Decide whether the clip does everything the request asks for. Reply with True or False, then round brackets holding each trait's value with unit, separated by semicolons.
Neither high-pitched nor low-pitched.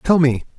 True (145 Hz)